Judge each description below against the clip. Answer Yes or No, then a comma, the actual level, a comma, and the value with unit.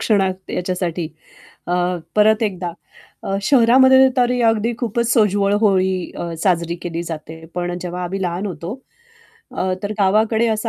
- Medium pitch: No, high, 195 Hz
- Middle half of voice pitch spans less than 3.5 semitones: No, average, 3.9 semitones